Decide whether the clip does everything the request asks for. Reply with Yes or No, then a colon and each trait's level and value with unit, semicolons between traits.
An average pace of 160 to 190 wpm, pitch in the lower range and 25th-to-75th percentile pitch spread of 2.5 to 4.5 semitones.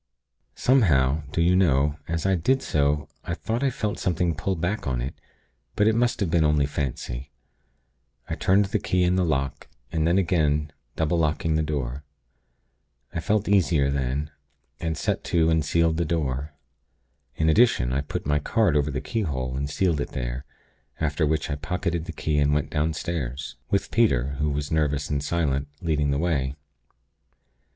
Yes: average, 175 wpm; very low, 75 Hz; average, 3.5 semitones